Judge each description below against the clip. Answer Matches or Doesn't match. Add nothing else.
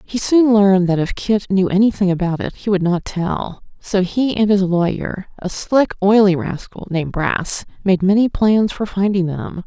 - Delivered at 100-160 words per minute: Doesn't match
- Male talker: Doesn't match